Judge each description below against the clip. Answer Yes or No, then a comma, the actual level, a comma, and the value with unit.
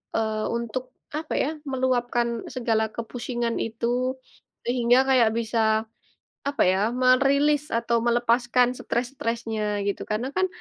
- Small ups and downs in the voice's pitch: Yes, narrow, 1.7 semitones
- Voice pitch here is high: Yes, high, 240 Hz